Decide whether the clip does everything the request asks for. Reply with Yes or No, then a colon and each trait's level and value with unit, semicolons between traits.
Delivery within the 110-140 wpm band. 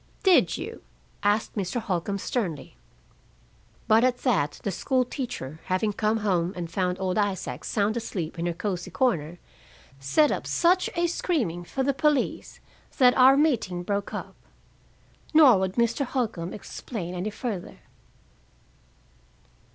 Yes: slow, 135 wpm